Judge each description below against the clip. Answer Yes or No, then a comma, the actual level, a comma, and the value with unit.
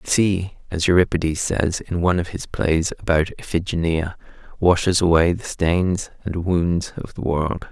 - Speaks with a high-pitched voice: No, very low, 85 Hz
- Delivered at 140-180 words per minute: Yes, average, 165 wpm